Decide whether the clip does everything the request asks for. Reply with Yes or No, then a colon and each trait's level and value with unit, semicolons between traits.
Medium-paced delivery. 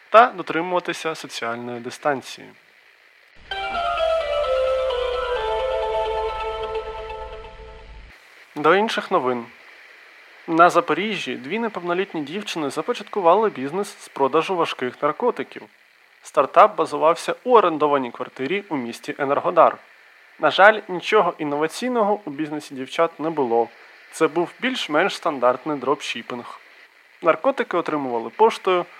No: slow, 90 wpm